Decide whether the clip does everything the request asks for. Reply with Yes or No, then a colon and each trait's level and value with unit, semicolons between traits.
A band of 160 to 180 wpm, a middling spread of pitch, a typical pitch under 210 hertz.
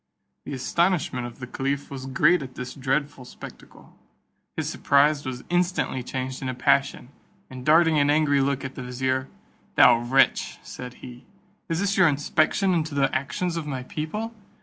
Yes: average, 165 wpm; average, 3.2 semitones; medium, 140 Hz